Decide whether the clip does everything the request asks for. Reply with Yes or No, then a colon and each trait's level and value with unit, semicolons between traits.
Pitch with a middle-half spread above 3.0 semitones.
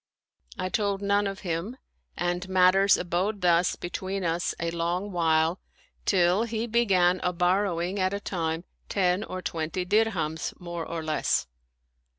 No: narrow, 2.5 semitones